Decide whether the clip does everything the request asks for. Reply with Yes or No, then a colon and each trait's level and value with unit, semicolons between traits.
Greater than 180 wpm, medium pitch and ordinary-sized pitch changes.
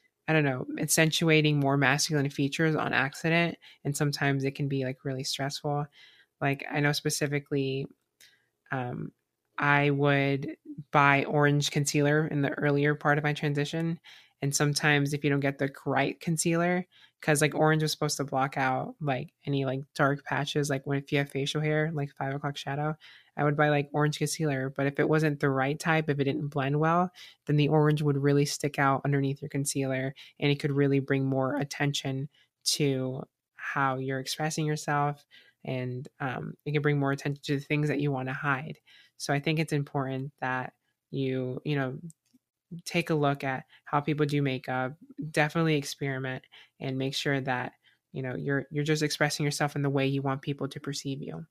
No: average, 190 wpm; medium, 145 Hz; narrow, 1.6 semitones